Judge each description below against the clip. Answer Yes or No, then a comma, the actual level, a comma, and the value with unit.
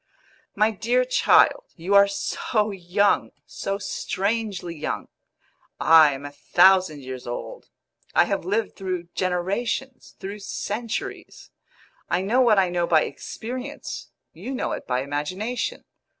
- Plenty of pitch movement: No, average, 4.7 semitones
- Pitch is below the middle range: No, high, 195 Hz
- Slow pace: Yes, slow, 130 wpm